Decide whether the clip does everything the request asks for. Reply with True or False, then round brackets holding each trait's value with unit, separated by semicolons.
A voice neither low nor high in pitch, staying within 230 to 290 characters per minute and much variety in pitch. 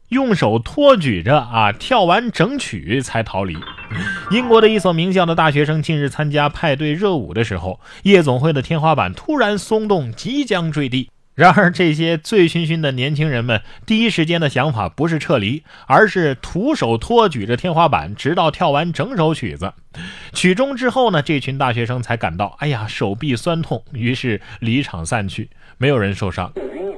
True (150 Hz; 270 characters per minute; 7.5 semitones)